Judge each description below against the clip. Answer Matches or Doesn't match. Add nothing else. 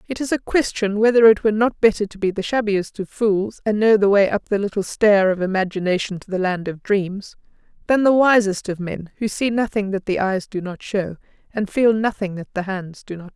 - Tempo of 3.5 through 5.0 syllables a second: Doesn't match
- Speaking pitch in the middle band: Doesn't match